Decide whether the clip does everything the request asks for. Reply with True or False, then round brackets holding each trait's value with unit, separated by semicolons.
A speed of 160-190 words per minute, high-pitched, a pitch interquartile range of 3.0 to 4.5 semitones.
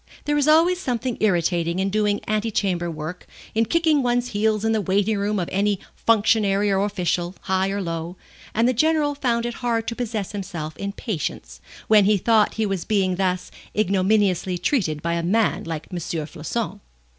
True (180 wpm; 205 Hz; 3.9 semitones)